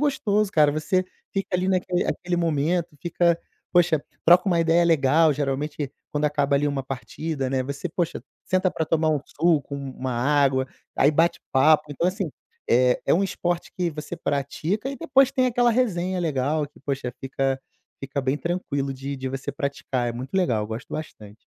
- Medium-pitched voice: Yes, medium, 150 Hz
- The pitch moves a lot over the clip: No, average, 4.4 semitones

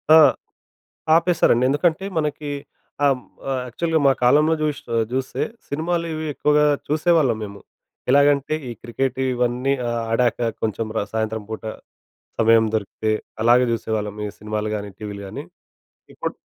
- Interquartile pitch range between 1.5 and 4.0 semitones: No, average, 5.1 semitones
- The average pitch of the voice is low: Yes, low, 125 Hz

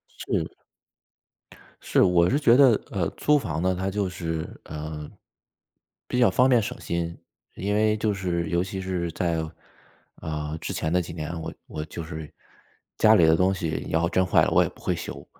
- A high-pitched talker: No, very low, 90 Hz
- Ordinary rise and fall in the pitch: Yes, average, 3.5 semitones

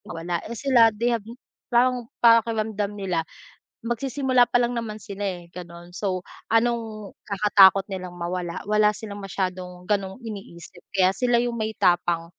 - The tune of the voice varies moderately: Yes, average, 4.1 semitones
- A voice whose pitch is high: Yes, high, 205 Hz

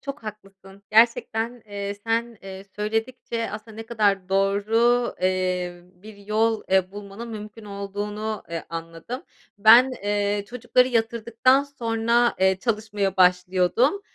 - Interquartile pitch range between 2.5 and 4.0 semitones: Yes, average, 2.8 semitones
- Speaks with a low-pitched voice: No, high, 210 Hz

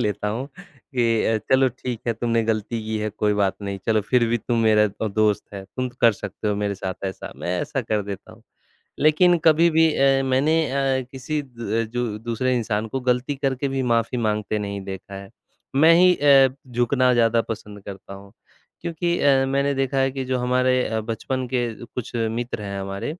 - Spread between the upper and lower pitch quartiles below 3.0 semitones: No, average, 3.8 semitones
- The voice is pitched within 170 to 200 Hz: No, low, 120 Hz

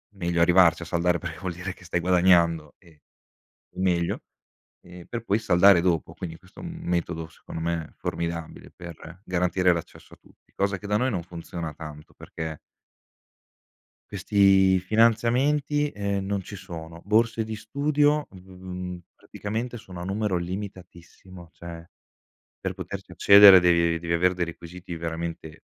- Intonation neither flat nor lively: Yes, average, 3.0 semitones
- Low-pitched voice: Yes, very low, 90 Hz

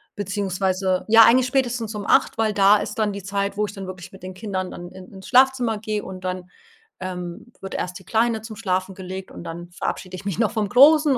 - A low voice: No, high, 200 Hz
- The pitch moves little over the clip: No, average, 3.1 semitones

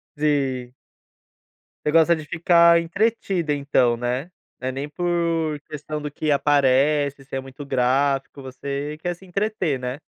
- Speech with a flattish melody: No, average, 3.6 semitones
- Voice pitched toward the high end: No, medium, 145 Hz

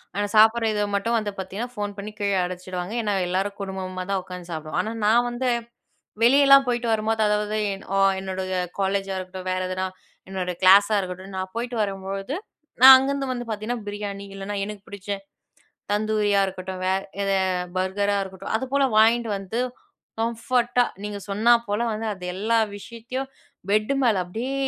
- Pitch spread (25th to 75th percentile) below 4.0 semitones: Yes, average, 3.3 semitones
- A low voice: No, high, 205 Hz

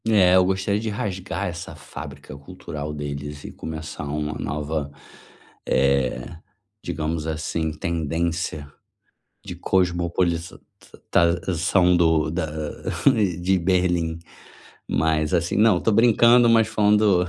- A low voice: Yes, very low, 85 Hz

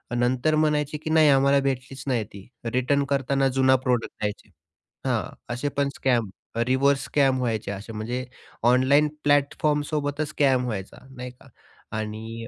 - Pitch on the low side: Yes, low, 130 Hz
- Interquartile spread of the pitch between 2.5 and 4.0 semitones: Yes, average, 2.9 semitones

